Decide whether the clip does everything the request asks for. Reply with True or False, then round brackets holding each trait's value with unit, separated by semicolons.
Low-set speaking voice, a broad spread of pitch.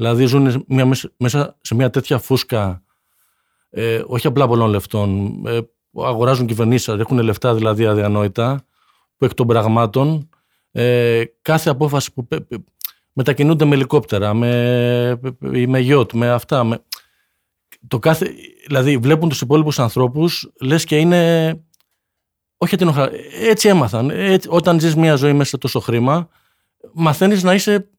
False (130 Hz; 5.0 semitones)